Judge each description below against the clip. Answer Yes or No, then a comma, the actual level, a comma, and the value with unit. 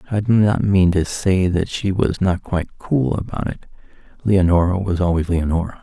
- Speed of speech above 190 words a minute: No, average, 185 wpm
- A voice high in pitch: No, very low, 95 Hz